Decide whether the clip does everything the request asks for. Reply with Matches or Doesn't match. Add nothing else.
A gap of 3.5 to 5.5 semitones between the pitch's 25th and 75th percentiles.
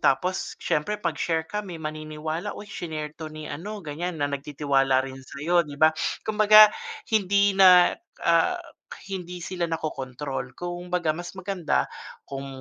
Matches